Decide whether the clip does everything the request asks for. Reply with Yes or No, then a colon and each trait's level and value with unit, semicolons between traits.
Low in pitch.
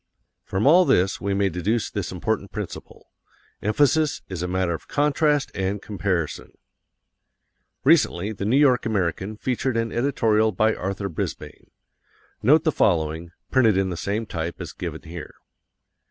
Yes: low, 105 Hz